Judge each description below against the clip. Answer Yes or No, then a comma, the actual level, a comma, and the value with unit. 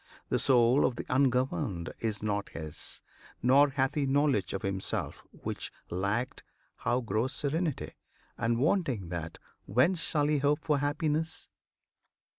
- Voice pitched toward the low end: Yes, low, 130 Hz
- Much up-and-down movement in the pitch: Yes, wide, 5.7 semitones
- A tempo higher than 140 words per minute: No, slow, 135 wpm